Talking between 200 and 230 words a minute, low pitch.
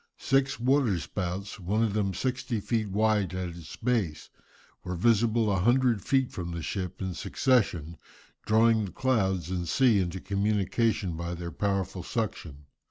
No: average, 155 wpm; low, 100 Hz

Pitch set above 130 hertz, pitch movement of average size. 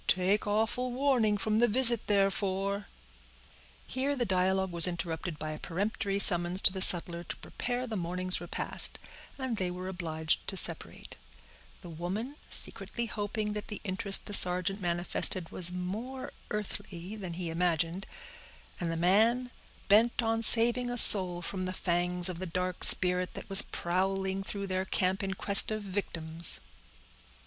Yes: high, 190 Hz; average, 3.1 semitones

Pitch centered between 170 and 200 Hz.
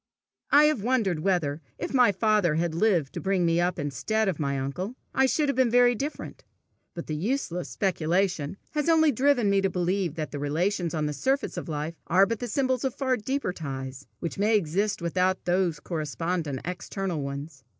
Yes: medium, 185 Hz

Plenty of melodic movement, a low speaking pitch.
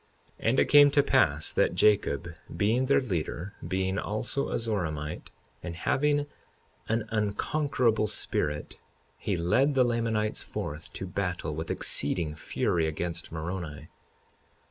Yes: wide, 6.2 semitones; low, 100 Hz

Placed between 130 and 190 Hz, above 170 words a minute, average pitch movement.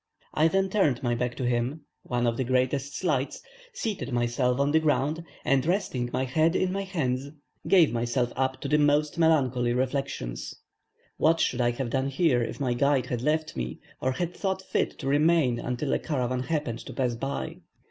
Yes: low, 135 Hz; average, 190 wpm; average, 4.1 semitones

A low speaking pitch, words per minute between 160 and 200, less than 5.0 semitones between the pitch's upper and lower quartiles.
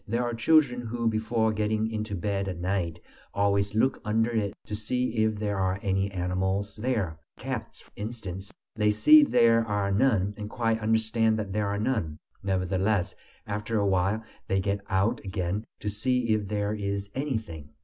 Yes: low, 105 Hz; average, 170 wpm; narrow, 2.4 semitones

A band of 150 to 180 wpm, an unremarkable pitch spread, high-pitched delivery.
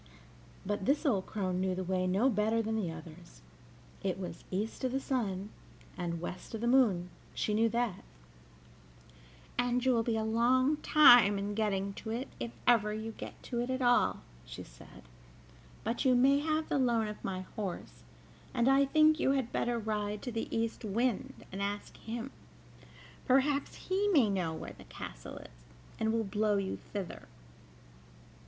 Yes: average, 175 wpm; average, 4.3 semitones; high, 220 Hz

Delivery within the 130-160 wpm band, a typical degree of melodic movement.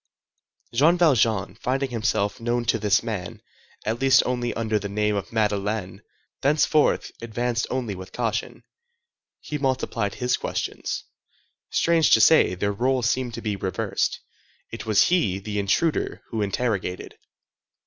Yes: average, 140 wpm; average, 3.7 semitones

